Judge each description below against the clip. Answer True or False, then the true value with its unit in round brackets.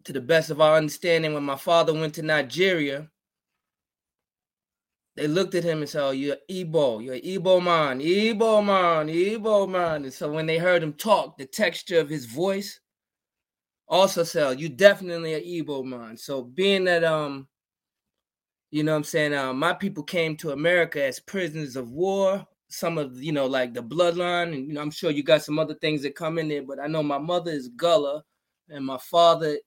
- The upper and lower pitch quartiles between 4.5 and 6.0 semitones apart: False (3.4 semitones)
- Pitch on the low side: False (160 Hz)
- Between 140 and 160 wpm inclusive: False (195 wpm)